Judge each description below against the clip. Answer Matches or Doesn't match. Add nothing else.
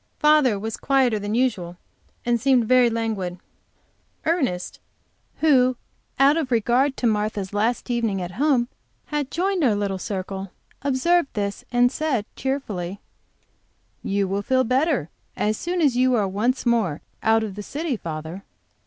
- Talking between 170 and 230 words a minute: Doesn't match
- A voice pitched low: Doesn't match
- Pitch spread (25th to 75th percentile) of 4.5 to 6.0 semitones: Matches